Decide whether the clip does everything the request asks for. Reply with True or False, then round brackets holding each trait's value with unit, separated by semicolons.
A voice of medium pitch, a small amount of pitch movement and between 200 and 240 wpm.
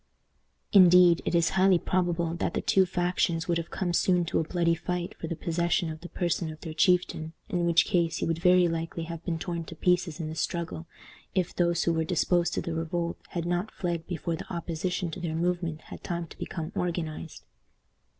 True (170 Hz; 1.4 semitones; 205 wpm)